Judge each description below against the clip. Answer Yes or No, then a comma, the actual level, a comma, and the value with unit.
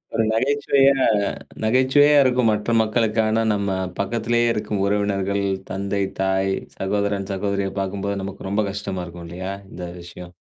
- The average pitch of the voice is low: Yes, low, 100 Hz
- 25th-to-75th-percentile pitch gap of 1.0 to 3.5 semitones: Yes, average, 2.7 semitones